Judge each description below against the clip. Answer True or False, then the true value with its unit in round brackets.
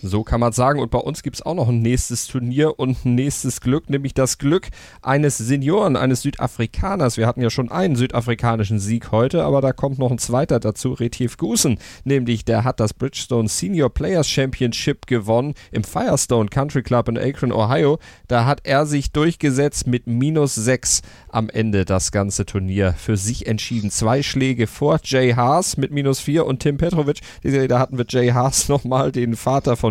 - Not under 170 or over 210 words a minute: True (190 wpm)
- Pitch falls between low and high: False (125 Hz)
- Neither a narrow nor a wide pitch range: True (3.2 semitones)